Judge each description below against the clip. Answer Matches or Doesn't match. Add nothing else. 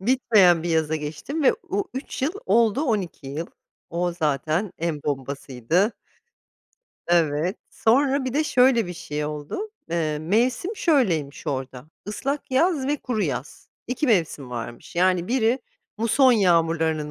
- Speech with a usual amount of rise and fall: Doesn't match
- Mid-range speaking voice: Matches